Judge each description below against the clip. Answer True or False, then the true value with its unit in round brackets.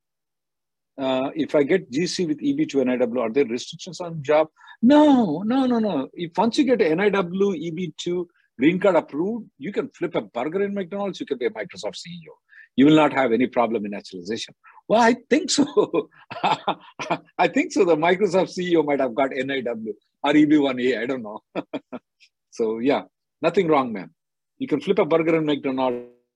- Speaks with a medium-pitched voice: True (175 Hz)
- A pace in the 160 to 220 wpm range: True (180 wpm)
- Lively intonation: True (8.2 semitones)